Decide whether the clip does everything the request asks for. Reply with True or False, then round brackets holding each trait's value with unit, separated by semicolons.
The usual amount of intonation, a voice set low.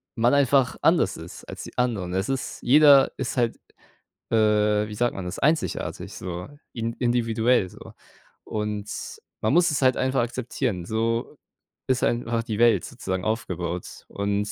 True (3.3 semitones; 115 Hz)